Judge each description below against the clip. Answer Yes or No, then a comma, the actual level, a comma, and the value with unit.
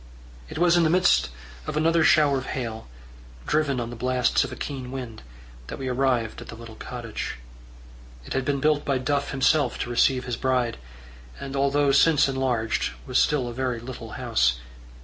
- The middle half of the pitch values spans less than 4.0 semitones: Yes, average, 2.9 semitones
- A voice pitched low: Yes, low, 130 Hz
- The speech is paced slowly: No, average, 185 wpm